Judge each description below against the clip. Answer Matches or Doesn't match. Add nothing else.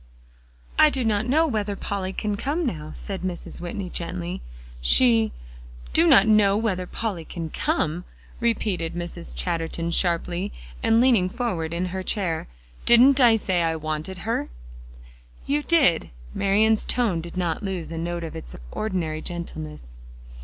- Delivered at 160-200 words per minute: Doesn't match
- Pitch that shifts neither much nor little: Matches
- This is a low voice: Doesn't match